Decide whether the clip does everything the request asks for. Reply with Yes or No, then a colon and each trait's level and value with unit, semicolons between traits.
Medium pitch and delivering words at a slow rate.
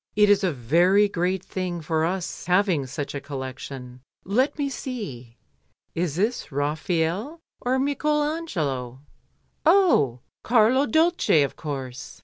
Yes: medium, 180 Hz; slow, 125 wpm